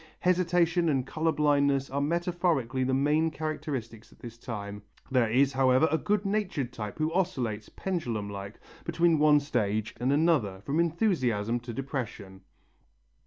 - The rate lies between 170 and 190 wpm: No, average, 145 wpm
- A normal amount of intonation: No, wide, 5.8 semitones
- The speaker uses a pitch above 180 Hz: No, medium, 140 Hz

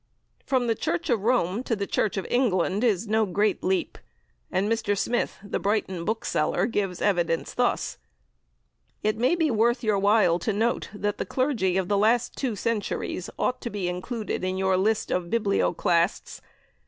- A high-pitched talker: Yes, high, 210 Hz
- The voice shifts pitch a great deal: No, average, 3.6 semitones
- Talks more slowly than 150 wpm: No, average, 170 wpm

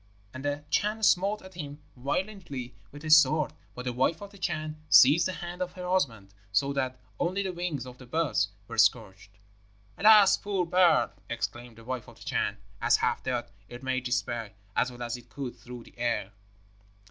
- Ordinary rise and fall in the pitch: No, wide, 6.6 semitones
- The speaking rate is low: No, average, 195 wpm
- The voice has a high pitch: No, medium, 140 Hz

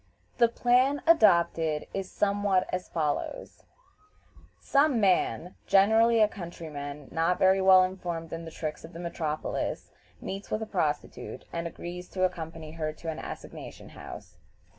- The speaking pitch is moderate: Yes, medium, 180 Hz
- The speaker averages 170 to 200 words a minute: No, average, 145 wpm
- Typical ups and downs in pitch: Yes, average, 3.7 semitones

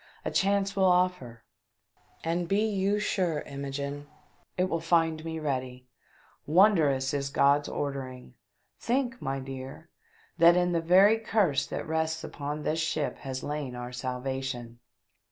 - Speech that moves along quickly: No, slow, 135 wpm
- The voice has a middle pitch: Yes, medium, 155 Hz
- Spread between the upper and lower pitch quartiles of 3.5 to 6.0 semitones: Yes, average, 5.0 semitones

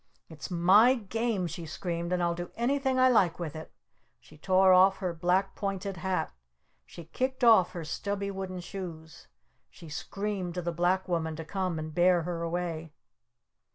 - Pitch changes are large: No, average, 2.8 semitones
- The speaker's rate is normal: Yes, average, 170 wpm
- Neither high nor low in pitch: Yes, medium, 180 Hz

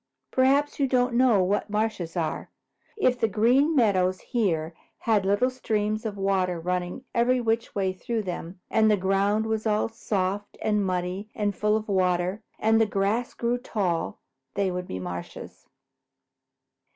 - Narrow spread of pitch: No, average, 3.5 semitones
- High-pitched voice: Yes, high, 210 Hz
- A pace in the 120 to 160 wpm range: Yes, average, 155 wpm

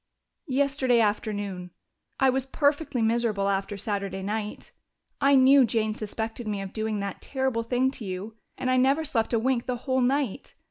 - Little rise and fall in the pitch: No, average, 4.1 semitones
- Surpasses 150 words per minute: Yes, average, 170 wpm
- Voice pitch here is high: Yes, high, 230 Hz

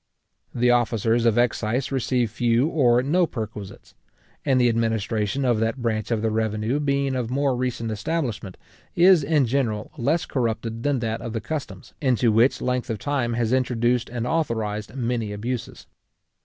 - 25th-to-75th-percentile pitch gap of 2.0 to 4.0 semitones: Yes, average, 2.8 semitones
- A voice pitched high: No, low, 120 Hz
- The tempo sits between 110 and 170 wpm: Yes, average, 160 wpm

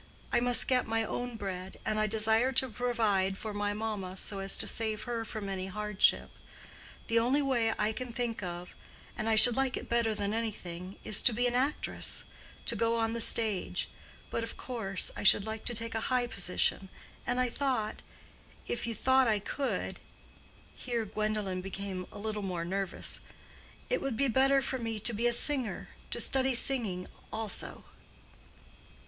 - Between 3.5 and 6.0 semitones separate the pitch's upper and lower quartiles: No, average, 3.1 semitones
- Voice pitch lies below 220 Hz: No, high, 225 Hz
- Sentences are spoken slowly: No, average, 165 wpm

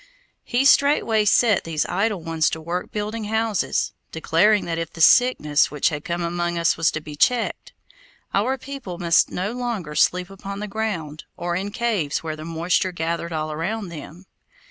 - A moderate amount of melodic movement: Yes, average, 4.8 semitones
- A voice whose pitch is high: No, medium, 175 Hz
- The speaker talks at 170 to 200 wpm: Yes, average, 175 wpm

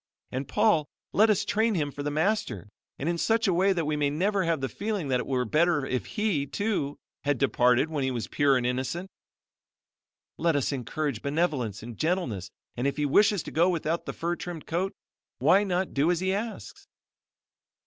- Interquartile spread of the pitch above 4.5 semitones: Yes, wide, 5.6 semitones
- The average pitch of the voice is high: No, medium, 155 Hz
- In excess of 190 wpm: Yes, average, 200 wpm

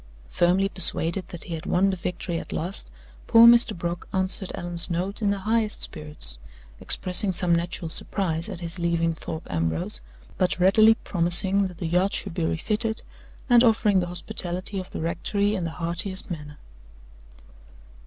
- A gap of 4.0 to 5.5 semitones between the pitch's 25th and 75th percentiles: No, average, 2.8 semitones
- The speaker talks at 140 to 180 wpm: Yes, average, 165 wpm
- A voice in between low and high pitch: Yes, medium, 180 Hz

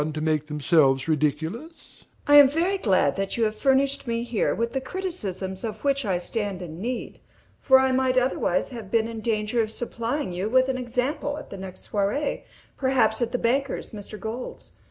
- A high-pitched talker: Yes, high, 235 Hz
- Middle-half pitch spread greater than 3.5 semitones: Yes, average, 4.0 semitones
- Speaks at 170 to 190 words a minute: Yes, average, 175 wpm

